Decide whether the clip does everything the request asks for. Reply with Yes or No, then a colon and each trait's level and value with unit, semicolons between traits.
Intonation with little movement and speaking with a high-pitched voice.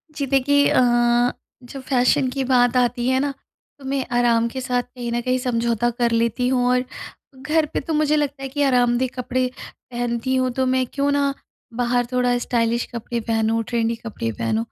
Yes: narrow, 2.0 semitones; very high, 250 Hz